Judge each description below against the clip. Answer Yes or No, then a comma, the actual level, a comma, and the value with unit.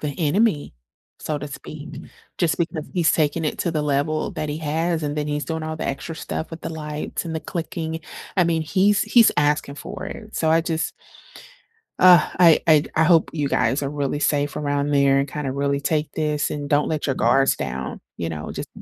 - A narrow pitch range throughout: Yes, narrow, 2.2 semitones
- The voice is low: No, medium, 150 Hz